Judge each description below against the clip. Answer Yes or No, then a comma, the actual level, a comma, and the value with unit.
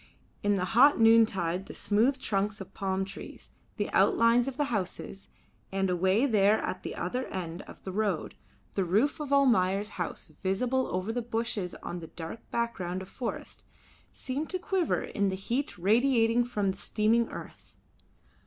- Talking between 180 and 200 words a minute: No, average, 165 wpm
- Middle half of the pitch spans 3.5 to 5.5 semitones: Yes, average, 4.2 semitones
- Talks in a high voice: Yes, high, 210 Hz